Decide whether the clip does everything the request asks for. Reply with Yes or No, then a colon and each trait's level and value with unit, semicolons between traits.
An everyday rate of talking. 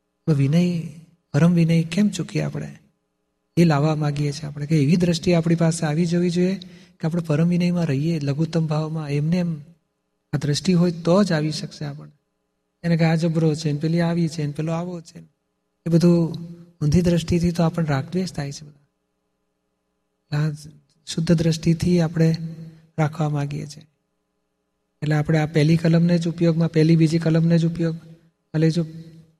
No: fast, 160 wpm